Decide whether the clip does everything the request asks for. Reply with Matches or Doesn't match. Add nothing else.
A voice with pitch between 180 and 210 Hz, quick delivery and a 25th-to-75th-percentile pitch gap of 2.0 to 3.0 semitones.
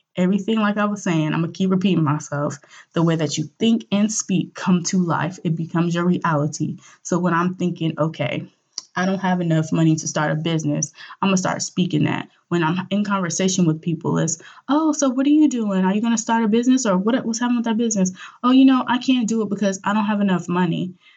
Doesn't match